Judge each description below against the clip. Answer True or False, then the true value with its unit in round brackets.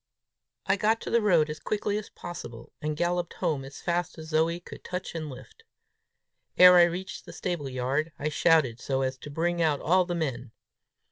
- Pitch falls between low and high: True (160 Hz)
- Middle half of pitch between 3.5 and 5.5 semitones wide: True (3.8 semitones)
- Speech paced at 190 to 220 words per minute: True (195 wpm)